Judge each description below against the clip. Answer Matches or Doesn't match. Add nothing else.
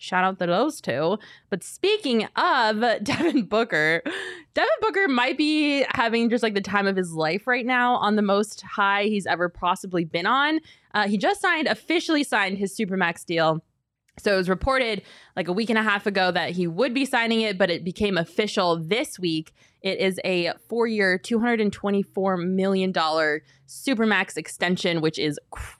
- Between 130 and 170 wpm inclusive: Doesn't match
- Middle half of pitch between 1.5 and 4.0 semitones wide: Doesn't match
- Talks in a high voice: Matches